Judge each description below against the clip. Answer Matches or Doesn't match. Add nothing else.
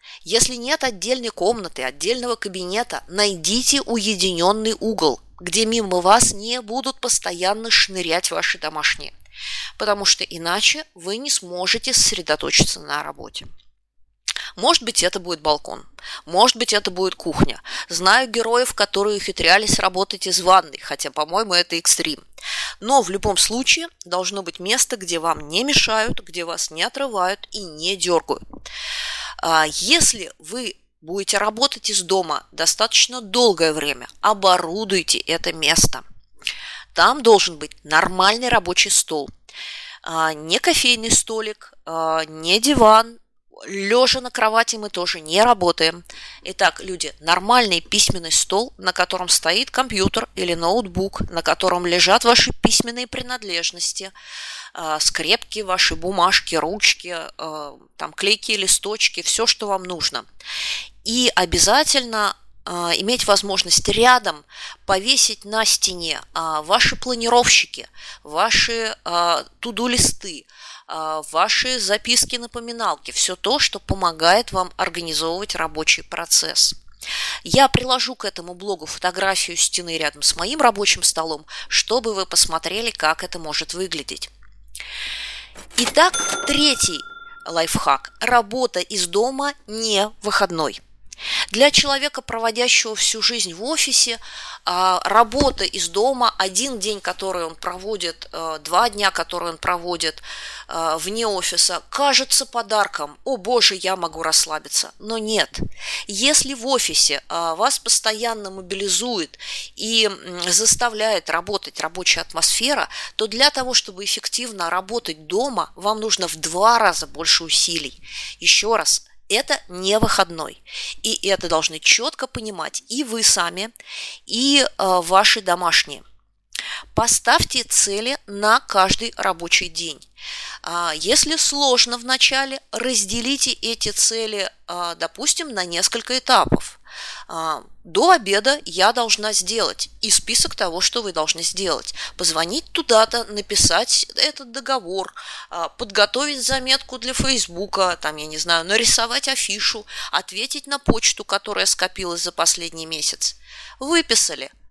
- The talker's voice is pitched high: Matches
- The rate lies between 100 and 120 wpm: Matches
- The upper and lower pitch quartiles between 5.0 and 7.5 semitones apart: Matches